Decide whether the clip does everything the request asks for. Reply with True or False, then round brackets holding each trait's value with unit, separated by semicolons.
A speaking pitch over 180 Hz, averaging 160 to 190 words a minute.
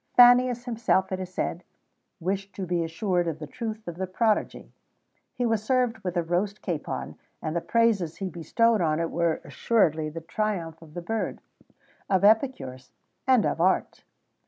True (190 Hz; 170 wpm)